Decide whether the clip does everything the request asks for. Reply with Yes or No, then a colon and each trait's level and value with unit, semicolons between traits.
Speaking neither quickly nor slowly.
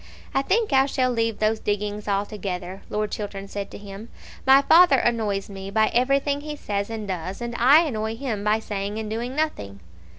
Yes: average, 190 wpm